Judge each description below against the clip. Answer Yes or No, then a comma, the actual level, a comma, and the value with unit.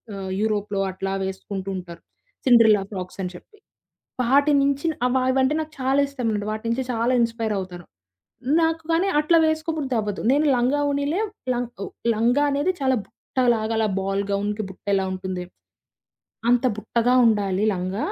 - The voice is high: Yes, high, 230 Hz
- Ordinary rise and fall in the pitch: No, wide, 5.8 semitones